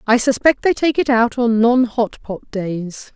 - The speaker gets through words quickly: Yes, fast, 210 wpm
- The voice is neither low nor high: No, high, 235 Hz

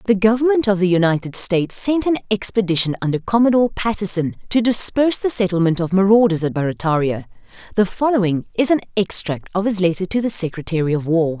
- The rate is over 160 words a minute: Yes, average, 175 wpm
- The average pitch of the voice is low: No, high, 195 Hz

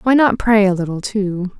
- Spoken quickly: Yes, fast, 225 wpm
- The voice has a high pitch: Yes, high, 205 Hz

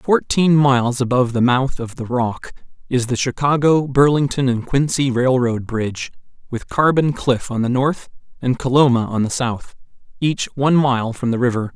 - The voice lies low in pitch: Yes, low, 130 Hz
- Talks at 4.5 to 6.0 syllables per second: Yes, 4.8 syllables/s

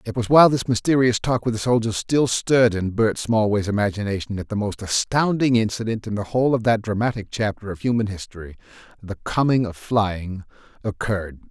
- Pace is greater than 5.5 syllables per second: Yes, 5.7 syllables/s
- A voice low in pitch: Yes, low, 110 Hz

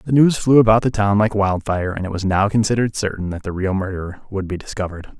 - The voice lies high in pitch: No, low, 100 Hz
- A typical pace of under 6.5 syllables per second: No, 6.7 syllables/s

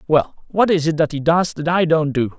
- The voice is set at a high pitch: No, medium, 155 Hz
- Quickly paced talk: Yes, fast, 275 wpm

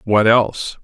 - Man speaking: Yes, male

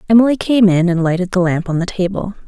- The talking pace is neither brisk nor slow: No, fast, 240 wpm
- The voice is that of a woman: Yes, female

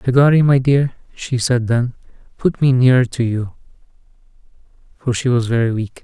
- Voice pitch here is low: Yes, low, 125 Hz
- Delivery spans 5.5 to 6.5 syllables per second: No, 5.1 syllables/s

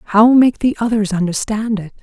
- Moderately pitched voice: No, high, 215 Hz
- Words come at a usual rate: Yes, average, 180 wpm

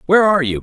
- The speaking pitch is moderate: Yes, medium, 170 Hz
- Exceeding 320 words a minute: No, fast, 290 wpm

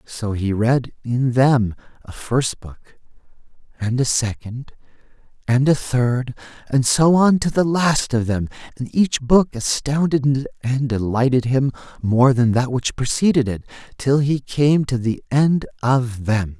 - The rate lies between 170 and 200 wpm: No, average, 155 wpm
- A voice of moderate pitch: No, low, 130 Hz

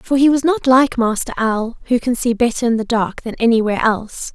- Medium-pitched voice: No, high, 235 Hz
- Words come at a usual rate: No, fast, 235 wpm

